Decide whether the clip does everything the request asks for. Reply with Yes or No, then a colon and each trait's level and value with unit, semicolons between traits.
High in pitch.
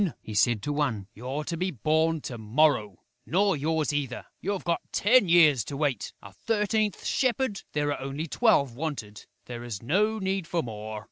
No: medium, 150 Hz